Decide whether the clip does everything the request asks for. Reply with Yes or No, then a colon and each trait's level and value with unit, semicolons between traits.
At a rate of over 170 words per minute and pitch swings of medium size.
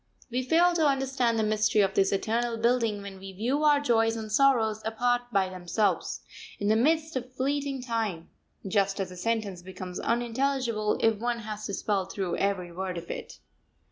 Yes: average, 180 wpm; average, 4.1 semitones